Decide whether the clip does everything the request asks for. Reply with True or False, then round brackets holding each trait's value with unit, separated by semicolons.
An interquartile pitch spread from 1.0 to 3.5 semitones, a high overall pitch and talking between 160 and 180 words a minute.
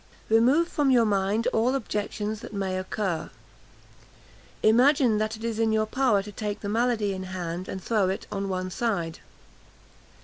True (3.1 semitones; 215 Hz; 165 wpm)